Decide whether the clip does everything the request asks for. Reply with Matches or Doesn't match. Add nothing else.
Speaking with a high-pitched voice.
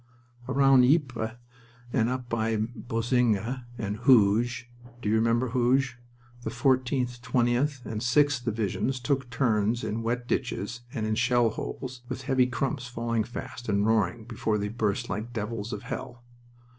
Doesn't match